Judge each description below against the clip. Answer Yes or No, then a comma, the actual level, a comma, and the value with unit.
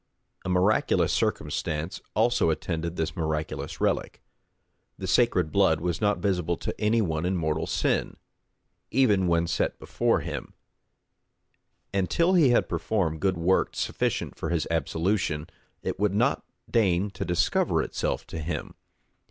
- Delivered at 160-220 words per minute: No, average, 140 wpm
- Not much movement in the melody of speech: No, average, 4.1 semitones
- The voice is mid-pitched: No, very low, 90 Hz